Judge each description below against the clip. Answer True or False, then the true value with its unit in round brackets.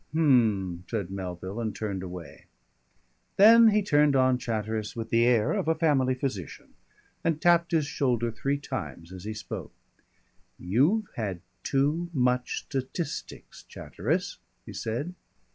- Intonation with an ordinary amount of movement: False (5.9 semitones)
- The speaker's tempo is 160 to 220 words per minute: False (135 wpm)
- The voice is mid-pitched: False (125 Hz)